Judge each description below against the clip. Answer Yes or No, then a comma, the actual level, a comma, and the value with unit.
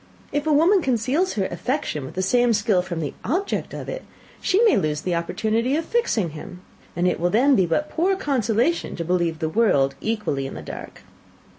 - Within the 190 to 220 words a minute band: Yes, average, 200 wpm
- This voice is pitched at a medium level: No, high, 220 Hz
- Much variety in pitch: Yes, wide, 9.0 semitones